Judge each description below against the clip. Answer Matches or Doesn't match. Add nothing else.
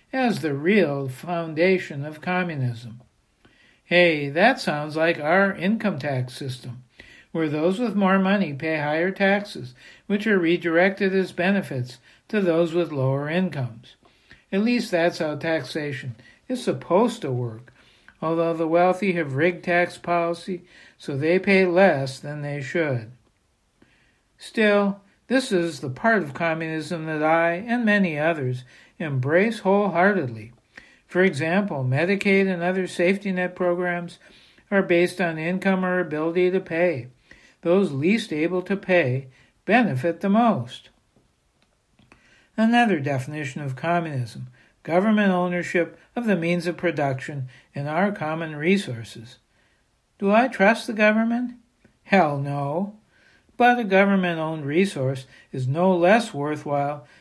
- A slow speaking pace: Matches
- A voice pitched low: Doesn't match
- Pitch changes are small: Doesn't match